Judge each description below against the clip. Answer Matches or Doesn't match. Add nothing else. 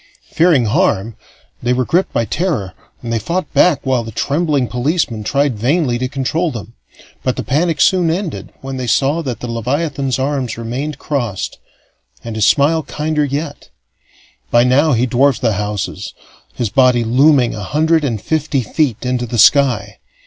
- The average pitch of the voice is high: Doesn't match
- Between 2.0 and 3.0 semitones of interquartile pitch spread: Doesn't match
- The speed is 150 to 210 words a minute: Matches